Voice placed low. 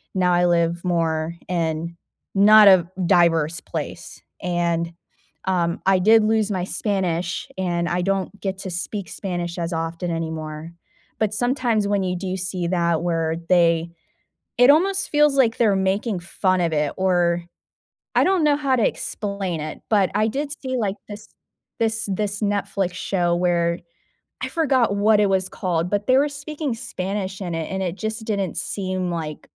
No: medium, 185 Hz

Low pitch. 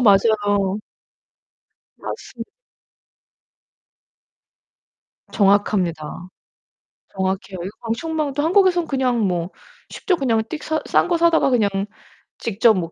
No: high, 225 Hz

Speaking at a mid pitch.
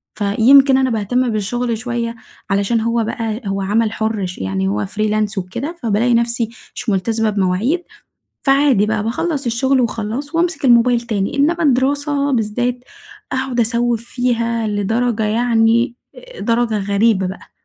No: high, 230 Hz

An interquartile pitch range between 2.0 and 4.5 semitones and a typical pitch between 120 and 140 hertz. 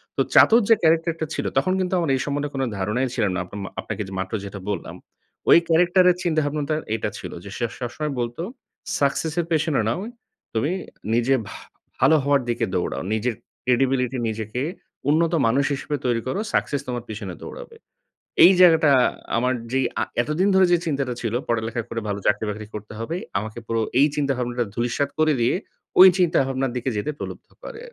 No: average, 5.3 semitones; low, 135 Hz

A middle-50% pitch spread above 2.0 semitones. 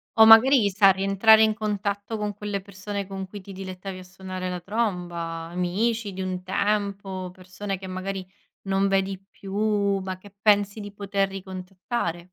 No: narrow, 1.7 semitones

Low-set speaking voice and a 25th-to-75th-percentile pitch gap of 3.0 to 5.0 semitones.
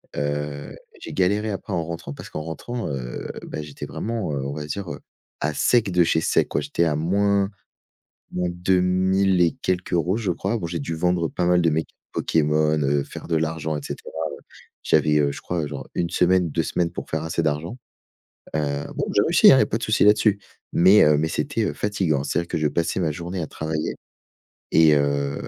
Yes: very low, 85 Hz; average, 3.4 semitones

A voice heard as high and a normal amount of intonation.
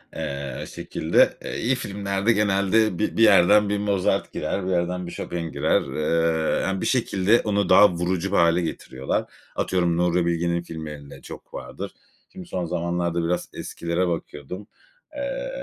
No: very low, 90 Hz; average, 3.0 semitones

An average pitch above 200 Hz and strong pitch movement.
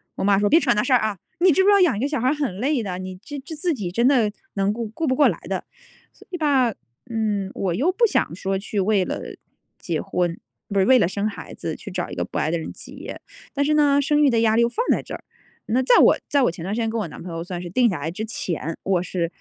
Yes: high, 220 Hz; wide, 6.9 semitones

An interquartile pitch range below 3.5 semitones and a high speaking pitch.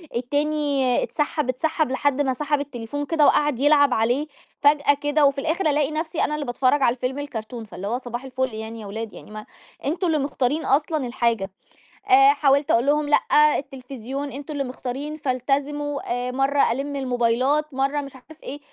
Yes: average, 2.9 semitones; very high, 275 Hz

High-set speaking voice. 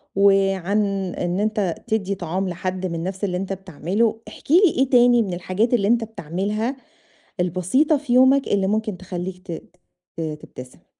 Yes: high, 195 Hz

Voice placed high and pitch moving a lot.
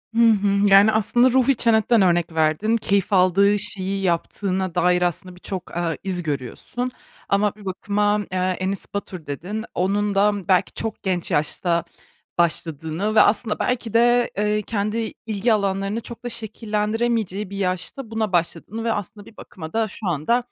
No: high, 200 Hz; average, 3.2 semitones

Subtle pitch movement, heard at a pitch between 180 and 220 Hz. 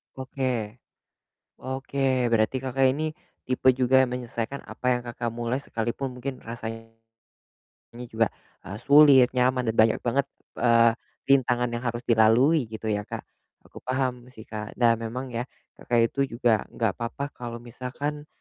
No: narrow, 2.3 semitones; low, 125 Hz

